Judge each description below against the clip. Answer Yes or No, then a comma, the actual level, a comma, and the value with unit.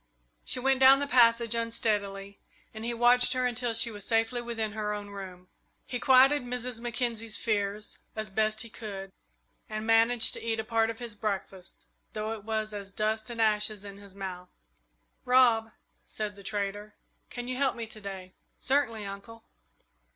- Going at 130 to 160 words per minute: No, average, 175 wpm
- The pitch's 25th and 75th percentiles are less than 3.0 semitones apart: Yes, narrow, 2.6 semitones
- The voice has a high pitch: Yes, high, 220 Hz